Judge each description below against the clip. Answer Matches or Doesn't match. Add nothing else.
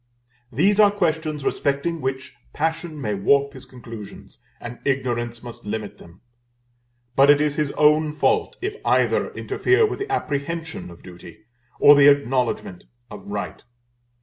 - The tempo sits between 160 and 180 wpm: Doesn't match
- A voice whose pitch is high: Doesn't match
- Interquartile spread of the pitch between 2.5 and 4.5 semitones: Doesn't match